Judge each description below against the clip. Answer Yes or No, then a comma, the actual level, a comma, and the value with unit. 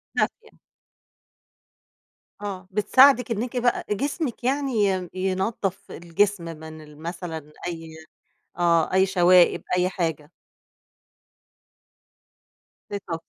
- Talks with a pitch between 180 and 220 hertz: Yes, medium, 185 Hz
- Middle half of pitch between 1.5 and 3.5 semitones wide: No, average, 4.0 semitones